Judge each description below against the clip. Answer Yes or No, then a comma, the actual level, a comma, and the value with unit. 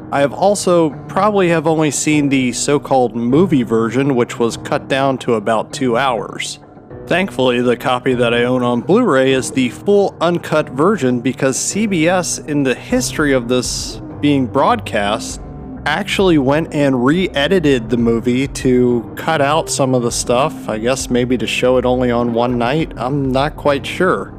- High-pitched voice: No, low, 130 Hz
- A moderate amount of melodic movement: Yes, average, 3.4 semitones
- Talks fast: No, average, 165 wpm